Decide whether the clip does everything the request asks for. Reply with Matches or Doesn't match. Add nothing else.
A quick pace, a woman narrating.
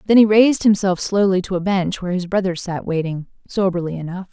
Matches